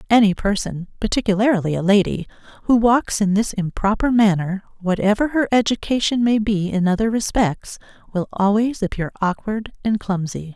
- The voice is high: Yes, high, 210 Hz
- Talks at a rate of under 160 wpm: Yes, average, 140 wpm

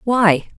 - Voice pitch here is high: Yes, high, 205 Hz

